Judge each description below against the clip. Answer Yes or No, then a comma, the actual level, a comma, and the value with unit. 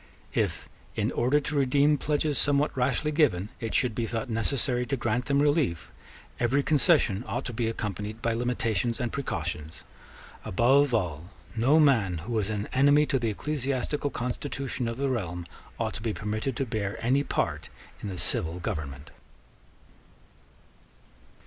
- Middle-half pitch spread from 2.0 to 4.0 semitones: No, average, 4.9 semitones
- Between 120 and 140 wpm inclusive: No, average, 155 wpm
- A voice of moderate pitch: No, low, 120 Hz